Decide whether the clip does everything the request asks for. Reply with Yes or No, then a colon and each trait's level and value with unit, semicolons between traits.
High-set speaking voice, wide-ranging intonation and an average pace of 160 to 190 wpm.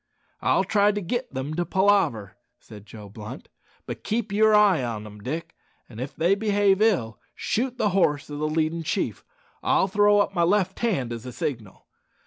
No: medium, 170 Hz; wide, 8.6 semitones; average, 185 wpm